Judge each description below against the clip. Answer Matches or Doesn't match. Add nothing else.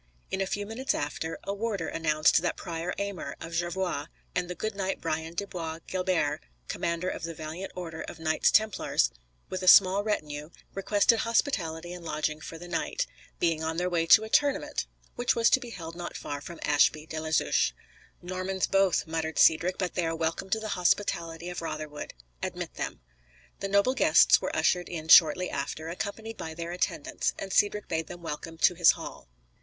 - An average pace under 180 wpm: Doesn't match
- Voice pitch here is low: Doesn't match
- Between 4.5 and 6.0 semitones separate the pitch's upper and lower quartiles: Doesn't match